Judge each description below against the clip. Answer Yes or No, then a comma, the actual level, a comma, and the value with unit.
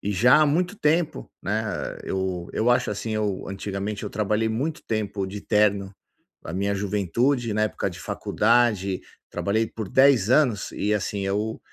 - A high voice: No, low, 105 Hz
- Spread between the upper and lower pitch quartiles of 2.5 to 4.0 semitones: Yes, average, 3.2 semitones